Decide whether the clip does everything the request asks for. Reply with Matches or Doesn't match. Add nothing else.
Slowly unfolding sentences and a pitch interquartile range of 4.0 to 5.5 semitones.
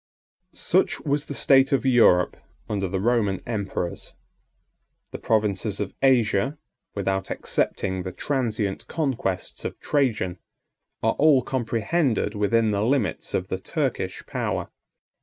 Matches